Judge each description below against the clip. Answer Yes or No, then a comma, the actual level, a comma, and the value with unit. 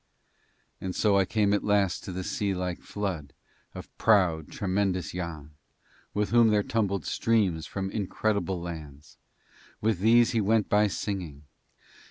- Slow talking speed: No, average, 145 wpm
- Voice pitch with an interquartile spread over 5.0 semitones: No, average, 3.0 semitones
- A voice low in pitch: Yes, low, 100 Hz